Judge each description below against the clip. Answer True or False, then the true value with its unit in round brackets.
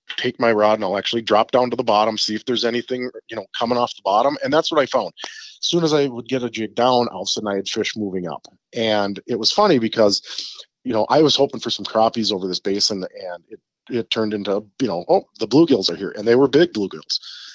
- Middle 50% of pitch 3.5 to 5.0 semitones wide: False (2.9 semitones)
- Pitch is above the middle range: False (110 Hz)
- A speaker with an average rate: False (265 wpm)